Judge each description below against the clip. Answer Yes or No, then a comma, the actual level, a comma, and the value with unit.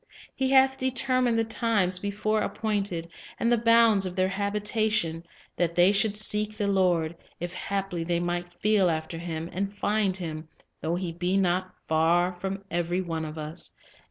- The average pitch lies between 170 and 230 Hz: Yes, high, 190 Hz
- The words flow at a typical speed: Yes, average, 165 wpm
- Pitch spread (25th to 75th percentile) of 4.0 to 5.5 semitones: No, average, 3.5 semitones